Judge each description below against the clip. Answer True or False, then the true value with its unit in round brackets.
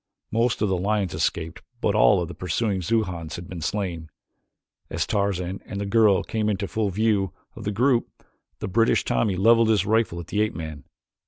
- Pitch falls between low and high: False (100 Hz)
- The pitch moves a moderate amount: True (3.5 semitones)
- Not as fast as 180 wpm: False (190 wpm)